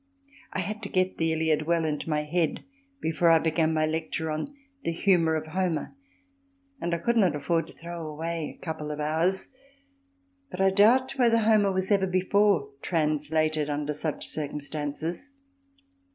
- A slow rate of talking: No, average, 165 wpm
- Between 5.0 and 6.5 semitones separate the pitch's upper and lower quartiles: No, average, 3.4 semitones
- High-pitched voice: No, medium, 165 Hz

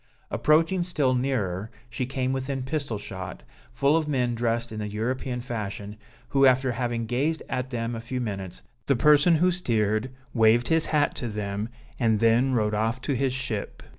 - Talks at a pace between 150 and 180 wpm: Yes, average, 175 wpm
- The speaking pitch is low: Yes, low, 120 Hz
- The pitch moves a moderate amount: Yes, average, 3.6 semitones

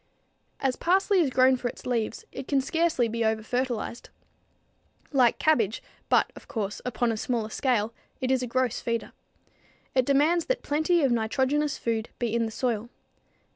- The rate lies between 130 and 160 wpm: No, average, 170 wpm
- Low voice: No, very high, 250 Hz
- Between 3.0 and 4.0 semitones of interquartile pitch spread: Yes, average, 3.4 semitones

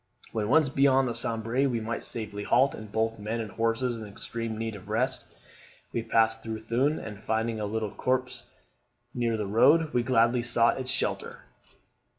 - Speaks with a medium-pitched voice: No, low, 115 Hz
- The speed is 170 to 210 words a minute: Yes, average, 180 wpm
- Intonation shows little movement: Yes, narrow, 2.2 semitones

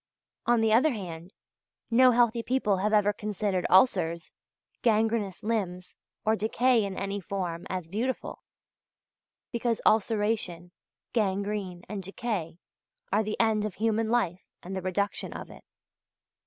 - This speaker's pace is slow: Yes, slow, 130 wpm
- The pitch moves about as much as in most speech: Yes, average, 3.3 semitones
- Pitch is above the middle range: Yes, high, 210 Hz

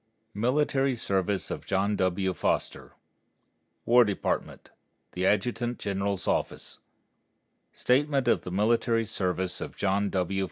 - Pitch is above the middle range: No, low, 100 Hz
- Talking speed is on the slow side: Yes, slow, 115 wpm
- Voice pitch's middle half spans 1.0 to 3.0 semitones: No, average, 4.1 semitones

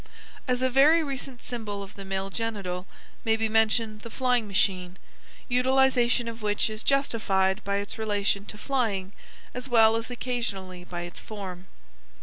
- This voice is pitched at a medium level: No, high, 220 Hz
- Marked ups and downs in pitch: No, average, 4.0 semitones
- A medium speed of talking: Yes, average, 155 wpm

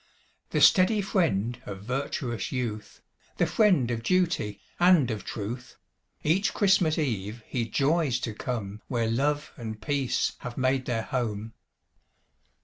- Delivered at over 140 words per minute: No, slow, 135 wpm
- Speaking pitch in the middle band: No, low, 125 Hz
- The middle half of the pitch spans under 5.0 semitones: No, wide, 5.4 semitones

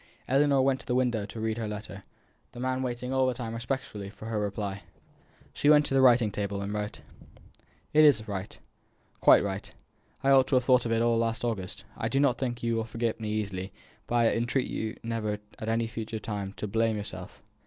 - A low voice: Yes, low, 115 Hz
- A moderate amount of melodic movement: Yes, average, 3.1 semitones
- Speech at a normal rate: No, fast, 215 wpm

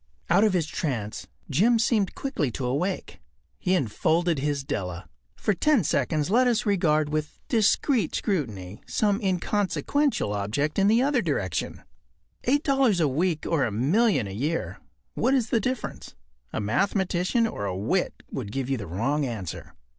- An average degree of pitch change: No, wide, 8.5 semitones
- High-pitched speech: No, medium, 170 Hz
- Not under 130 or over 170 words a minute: Yes, average, 160 wpm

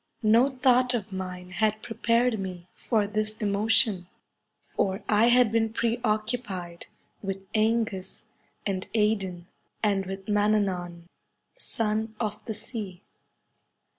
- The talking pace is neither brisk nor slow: No, slow, 115 wpm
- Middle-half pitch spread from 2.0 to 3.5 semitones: Yes, average, 2.8 semitones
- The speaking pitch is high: Yes, high, 215 Hz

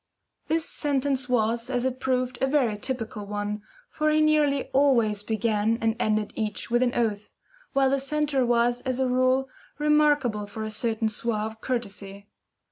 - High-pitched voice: Yes, high, 245 Hz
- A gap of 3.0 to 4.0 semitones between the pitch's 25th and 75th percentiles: Yes, average, 3.6 semitones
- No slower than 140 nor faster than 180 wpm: Yes, average, 160 wpm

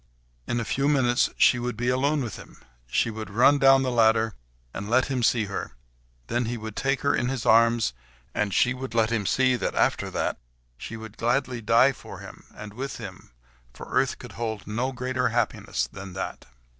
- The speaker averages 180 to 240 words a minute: Yes, average, 200 wpm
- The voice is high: No, low, 120 Hz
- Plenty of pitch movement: No, average, 2.7 semitones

